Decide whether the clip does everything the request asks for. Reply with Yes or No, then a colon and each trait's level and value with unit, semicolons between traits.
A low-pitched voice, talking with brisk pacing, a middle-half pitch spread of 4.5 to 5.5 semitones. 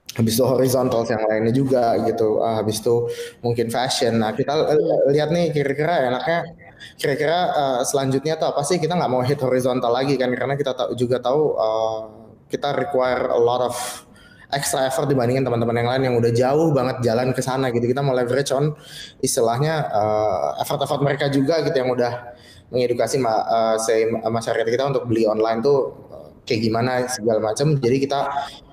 No: low, 125 Hz; fast, 180 wpm; average, 3.3 semitones